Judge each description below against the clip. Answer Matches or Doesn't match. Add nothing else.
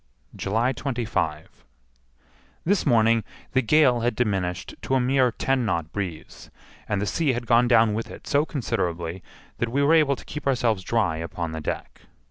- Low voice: Matches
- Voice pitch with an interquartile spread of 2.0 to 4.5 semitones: Doesn't match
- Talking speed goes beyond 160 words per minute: Matches